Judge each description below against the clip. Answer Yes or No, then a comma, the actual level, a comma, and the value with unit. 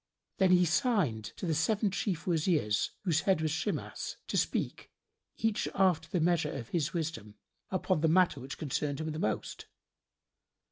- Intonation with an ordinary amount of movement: Yes, average, 3.6 semitones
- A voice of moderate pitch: Yes, medium, 165 Hz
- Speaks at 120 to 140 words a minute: No, average, 160 wpm